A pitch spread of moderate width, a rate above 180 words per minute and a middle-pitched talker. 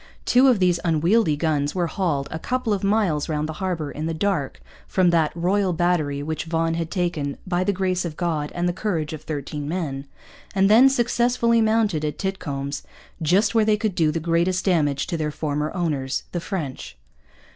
Yes: average, 4.2 semitones; average, 190 wpm; medium, 170 Hz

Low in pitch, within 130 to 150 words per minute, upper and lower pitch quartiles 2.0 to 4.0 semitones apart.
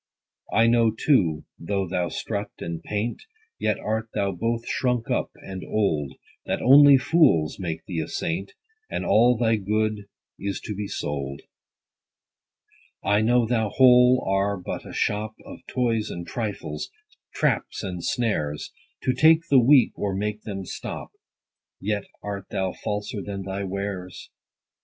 Yes: low, 105 Hz; average, 145 wpm; average, 3.5 semitones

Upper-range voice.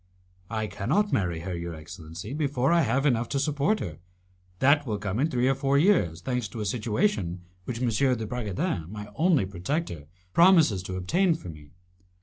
No: low, 115 Hz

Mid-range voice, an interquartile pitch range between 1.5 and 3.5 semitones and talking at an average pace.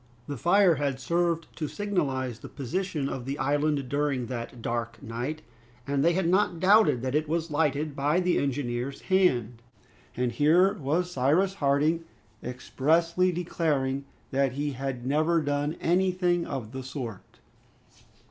No: medium, 145 Hz; average, 4.4 semitones; average, 145 wpm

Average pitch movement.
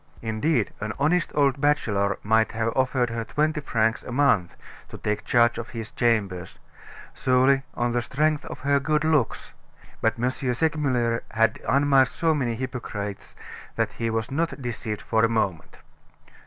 Yes: average, 4.0 semitones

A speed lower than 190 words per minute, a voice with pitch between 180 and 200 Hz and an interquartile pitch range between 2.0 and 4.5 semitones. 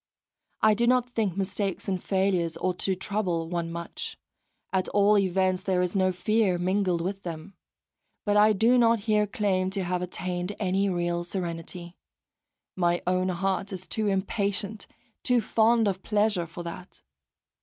Yes: average, 155 wpm; high, 190 Hz; narrow, 2.6 semitones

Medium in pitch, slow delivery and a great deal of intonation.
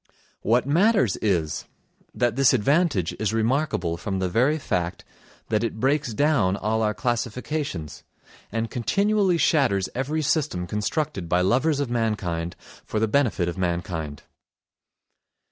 No: low, 115 Hz; slow, 130 wpm; wide, 7.2 semitones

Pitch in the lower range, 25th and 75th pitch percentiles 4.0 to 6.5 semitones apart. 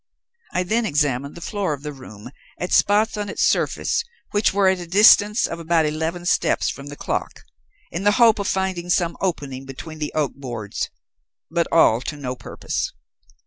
No: medium, 170 Hz; average, 5.3 semitones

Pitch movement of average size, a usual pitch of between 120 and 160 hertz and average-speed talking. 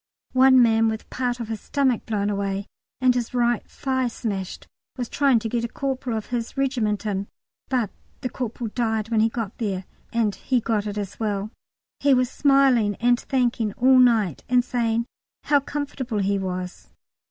No: average, 3.2 semitones; high, 235 Hz; average, 175 wpm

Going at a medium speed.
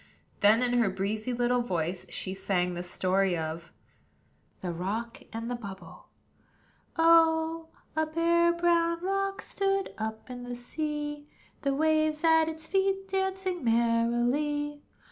No: slow, 130 wpm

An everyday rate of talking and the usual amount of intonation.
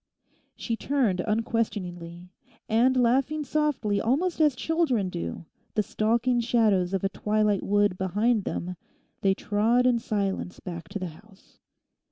No: slow, 130 wpm; average, 4.4 semitones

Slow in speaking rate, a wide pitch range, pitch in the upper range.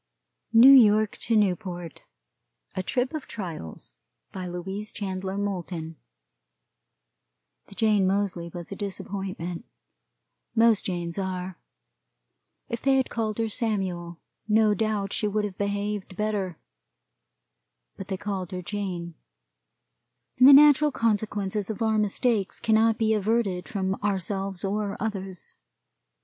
No: slow, 120 wpm; average, 2.7 semitones; high, 200 Hz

